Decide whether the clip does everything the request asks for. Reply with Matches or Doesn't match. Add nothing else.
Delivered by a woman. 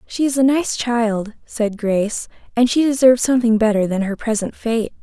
Matches